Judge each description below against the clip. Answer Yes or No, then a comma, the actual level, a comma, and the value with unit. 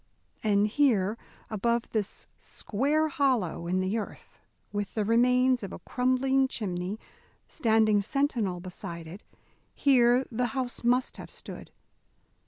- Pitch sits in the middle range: No, high, 230 Hz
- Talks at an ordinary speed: No, slow, 125 wpm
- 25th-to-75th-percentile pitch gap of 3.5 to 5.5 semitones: Yes, average, 4.2 semitones